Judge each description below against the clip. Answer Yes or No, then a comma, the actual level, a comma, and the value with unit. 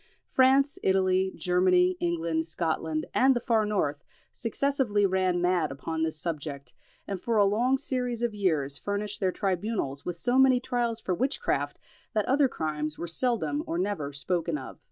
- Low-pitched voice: No, medium, 185 Hz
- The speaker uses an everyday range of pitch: No, wide, 6.3 semitones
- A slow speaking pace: No, average, 160 wpm